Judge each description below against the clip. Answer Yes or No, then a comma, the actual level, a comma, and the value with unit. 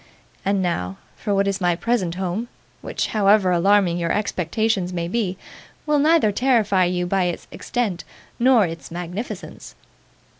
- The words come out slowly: No, average, 145 wpm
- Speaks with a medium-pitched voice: No, high, 195 Hz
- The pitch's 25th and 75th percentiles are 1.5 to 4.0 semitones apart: Yes, average, 3.6 semitones